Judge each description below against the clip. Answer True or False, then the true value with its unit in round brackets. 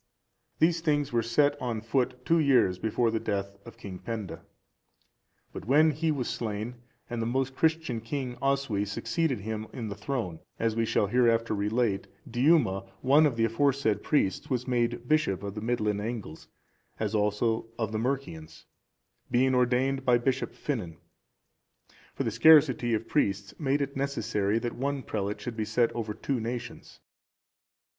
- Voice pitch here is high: False (120 Hz)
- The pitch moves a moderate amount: True (4.1 semitones)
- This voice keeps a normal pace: True (165 wpm)